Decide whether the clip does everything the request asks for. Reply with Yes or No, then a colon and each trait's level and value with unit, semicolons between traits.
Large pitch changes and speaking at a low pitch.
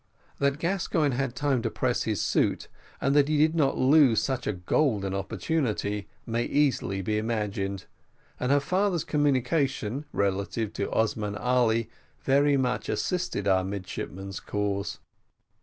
Yes: wide, 5.8 semitones; low, 125 Hz